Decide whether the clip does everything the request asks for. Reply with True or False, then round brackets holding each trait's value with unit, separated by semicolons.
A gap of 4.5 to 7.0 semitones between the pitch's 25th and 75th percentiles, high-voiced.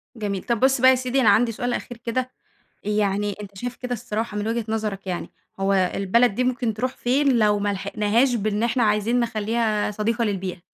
False (3.0 semitones; 220 Hz)